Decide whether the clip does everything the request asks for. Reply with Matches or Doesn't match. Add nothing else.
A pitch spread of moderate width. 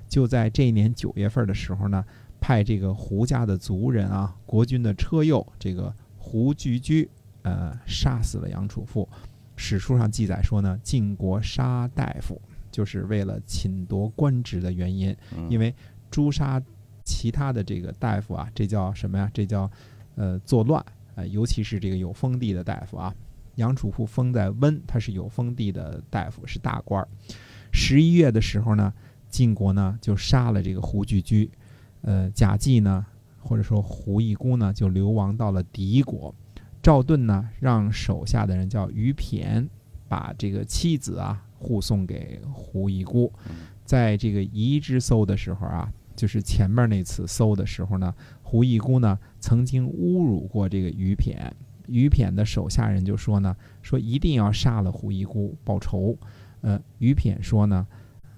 Matches